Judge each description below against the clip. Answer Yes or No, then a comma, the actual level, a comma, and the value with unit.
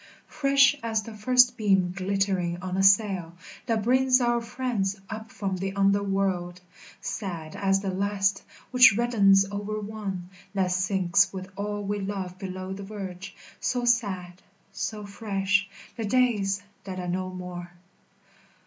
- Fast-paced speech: No, average, 145 wpm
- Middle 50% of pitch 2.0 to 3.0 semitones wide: Yes, narrow, 2.4 semitones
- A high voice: Yes, high, 195 Hz